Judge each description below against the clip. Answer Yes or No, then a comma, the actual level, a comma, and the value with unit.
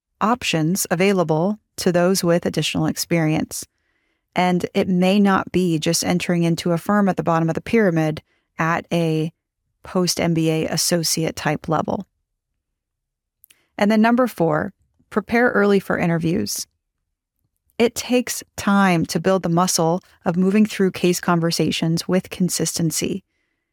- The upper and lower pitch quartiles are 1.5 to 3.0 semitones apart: Yes, average, 2.7 semitones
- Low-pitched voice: No, medium, 180 Hz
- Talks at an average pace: No, slow, 130 wpm